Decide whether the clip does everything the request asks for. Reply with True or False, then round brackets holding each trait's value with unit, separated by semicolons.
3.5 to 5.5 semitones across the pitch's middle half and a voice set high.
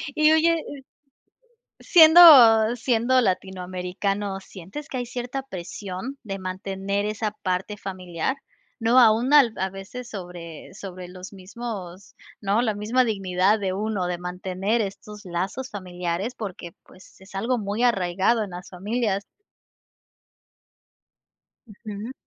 True (4.2 semitones; 200 Hz)